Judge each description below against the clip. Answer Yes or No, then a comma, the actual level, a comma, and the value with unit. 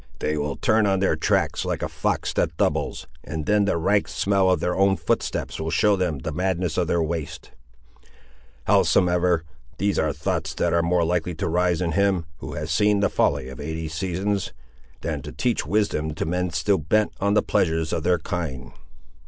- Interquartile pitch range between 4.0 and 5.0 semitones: No, average, 3.5 semitones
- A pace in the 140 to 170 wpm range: No, average, 195 wpm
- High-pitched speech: No, very low, 85 Hz